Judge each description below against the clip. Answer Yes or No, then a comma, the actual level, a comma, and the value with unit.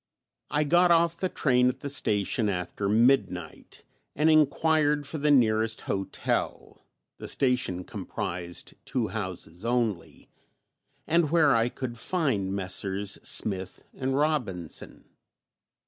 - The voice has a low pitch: Yes, low, 120 Hz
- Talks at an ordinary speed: No, slow, 115 wpm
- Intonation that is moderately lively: No, wide, 6.9 semitones